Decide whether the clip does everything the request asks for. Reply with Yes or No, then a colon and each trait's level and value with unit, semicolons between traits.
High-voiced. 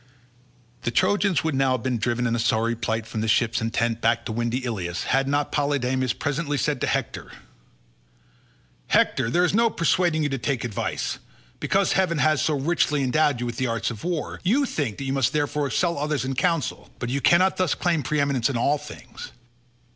No: low, 135 Hz